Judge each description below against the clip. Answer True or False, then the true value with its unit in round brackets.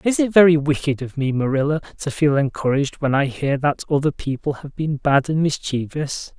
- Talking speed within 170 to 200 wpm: True (195 wpm)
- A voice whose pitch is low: False (145 Hz)